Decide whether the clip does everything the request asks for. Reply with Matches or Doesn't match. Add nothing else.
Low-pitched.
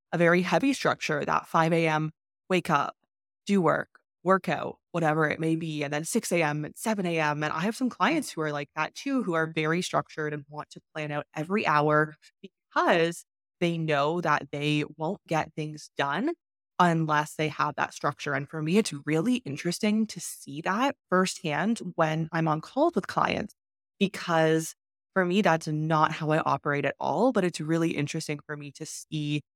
Doesn't match